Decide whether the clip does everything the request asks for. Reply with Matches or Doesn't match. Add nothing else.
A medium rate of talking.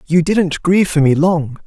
Doesn't match